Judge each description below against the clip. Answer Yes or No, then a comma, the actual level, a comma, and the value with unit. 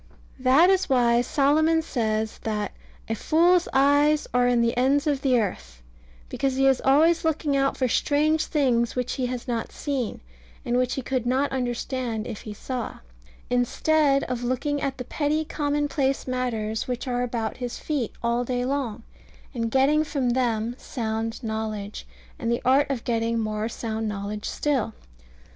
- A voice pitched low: No, very high, 250 Hz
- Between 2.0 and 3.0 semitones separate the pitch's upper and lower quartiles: No, average, 3.5 semitones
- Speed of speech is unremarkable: Yes, average, 165 wpm